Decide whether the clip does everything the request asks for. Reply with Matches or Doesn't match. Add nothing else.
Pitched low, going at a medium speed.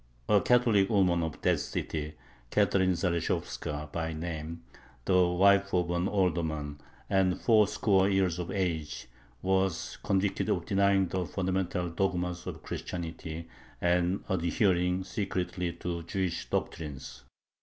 Doesn't match